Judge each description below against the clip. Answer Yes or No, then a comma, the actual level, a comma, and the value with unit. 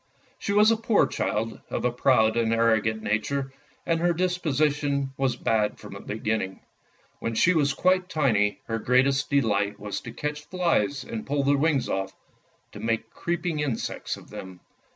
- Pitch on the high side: No, low, 135 Hz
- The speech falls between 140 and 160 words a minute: No, average, 170 wpm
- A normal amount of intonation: No, wide, 5.7 semitones